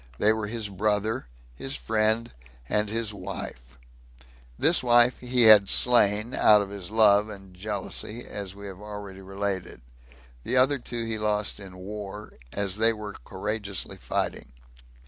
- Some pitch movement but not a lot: No, narrow, 2.0 semitones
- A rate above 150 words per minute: No, average, 145 wpm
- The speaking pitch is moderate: No, low, 105 Hz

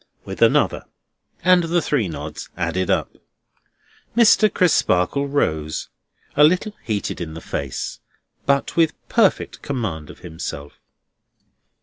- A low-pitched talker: Yes, low, 120 Hz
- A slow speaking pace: Yes, slow, 115 wpm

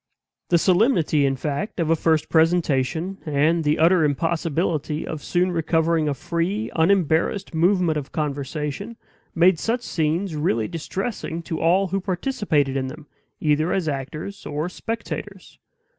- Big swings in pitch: No, average, 3.4 semitones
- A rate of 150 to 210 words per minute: No, average, 140 wpm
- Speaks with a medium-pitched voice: Yes, medium, 165 Hz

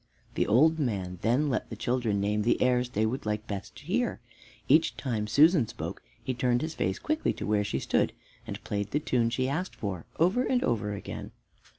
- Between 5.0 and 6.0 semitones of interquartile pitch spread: Yes, wide, 5.4 semitones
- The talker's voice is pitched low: Yes, low, 120 Hz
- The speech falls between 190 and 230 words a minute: Yes, fast, 205 wpm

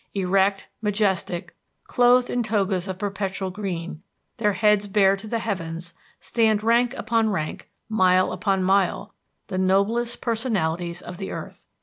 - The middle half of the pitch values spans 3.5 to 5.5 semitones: No, average, 2.9 semitones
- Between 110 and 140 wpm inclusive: Yes, slow, 135 wpm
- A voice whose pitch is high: Yes, high, 195 Hz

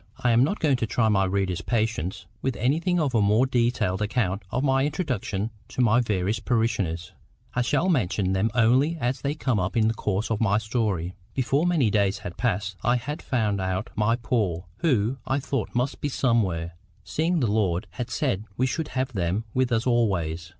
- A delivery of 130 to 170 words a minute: No, average, 195 wpm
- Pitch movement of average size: Yes, average, 4.7 semitones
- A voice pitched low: Yes, low, 115 Hz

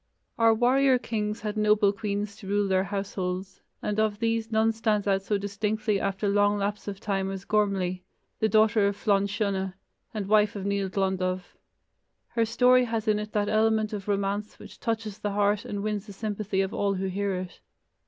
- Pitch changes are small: Yes, narrow, 1.7 semitones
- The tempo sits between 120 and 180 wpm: No, average, 190 wpm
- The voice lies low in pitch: No, high, 205 Hz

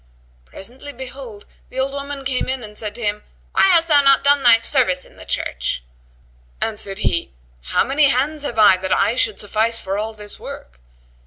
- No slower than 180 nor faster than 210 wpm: Yes, average, 190 wpm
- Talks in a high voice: Yes, high, 235 Hz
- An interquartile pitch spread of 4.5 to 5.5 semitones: Yes, average, 4.9 semitones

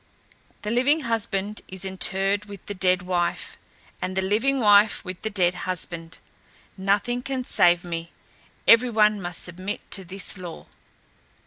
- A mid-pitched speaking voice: No, high, 195 Hz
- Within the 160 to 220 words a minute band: No, average, 145 wpm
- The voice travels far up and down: No, average, 2.7 semitones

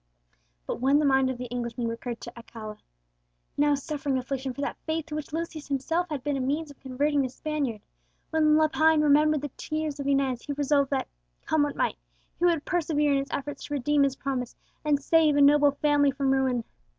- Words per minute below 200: No, fast, 205 wpm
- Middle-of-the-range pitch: No, very high, 285 Hz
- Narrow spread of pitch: Yes, narrow, 2.2 semitones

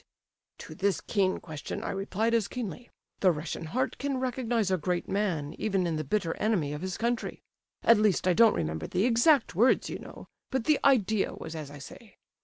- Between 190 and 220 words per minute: Yes, fast, 205 wpm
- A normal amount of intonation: No, wide, 5.7 semitones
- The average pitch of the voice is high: Yes, high, 200 Hz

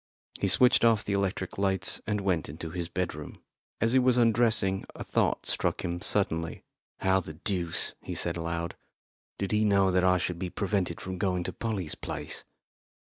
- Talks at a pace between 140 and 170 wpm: No, average, 180 wpm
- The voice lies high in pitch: No, very low, 95 Hz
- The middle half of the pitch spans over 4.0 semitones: No, average, 2.9 semitones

